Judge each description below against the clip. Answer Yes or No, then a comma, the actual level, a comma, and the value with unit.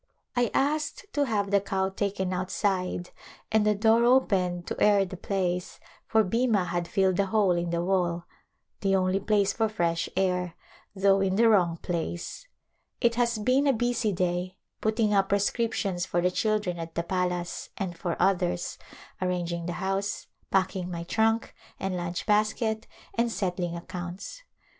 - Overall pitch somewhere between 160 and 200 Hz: Yes, high, 190 Hz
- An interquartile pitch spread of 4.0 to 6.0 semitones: No, average, 3.3 semitones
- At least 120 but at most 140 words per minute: No, average, 165 wpm